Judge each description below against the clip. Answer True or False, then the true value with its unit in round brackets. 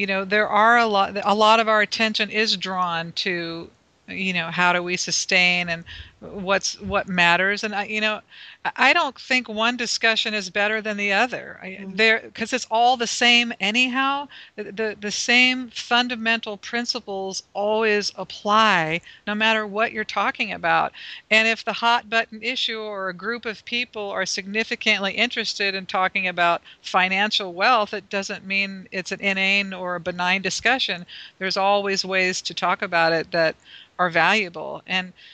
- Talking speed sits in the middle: True (165 wpm)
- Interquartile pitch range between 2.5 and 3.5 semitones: True (3.0 semitones)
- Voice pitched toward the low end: False (205 Hz)